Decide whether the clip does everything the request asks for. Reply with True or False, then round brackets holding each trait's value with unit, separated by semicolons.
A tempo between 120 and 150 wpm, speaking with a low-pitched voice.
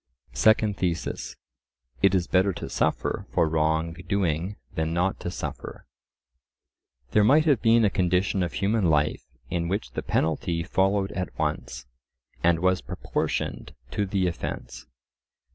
True (140 wpm; 90 Hz)